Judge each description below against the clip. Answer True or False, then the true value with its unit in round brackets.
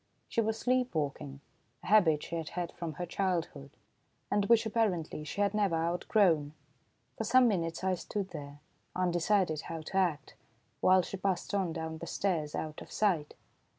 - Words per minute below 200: True (170 wpm)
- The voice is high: False (175 Hz)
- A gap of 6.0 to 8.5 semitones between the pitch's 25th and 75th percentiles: False (4.1 semitones)